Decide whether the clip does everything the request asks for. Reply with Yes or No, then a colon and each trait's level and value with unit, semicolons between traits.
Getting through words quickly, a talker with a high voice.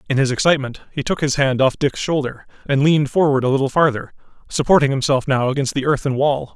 No: fast, 210 wpm; medium, 140 Hz